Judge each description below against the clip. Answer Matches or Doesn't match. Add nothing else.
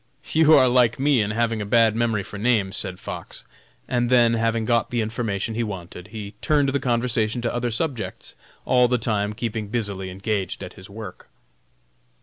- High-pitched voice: Doesn't match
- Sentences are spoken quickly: Doesn't match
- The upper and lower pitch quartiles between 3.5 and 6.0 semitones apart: Doesn't match